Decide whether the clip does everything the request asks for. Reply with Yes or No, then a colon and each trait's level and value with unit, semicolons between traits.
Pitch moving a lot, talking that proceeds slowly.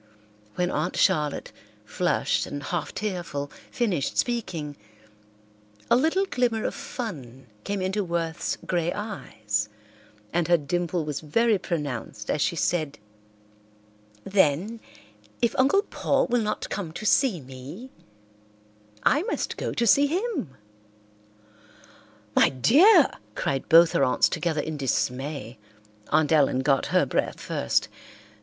Yes: wide, 7.7 semitones; slow, 125 wpm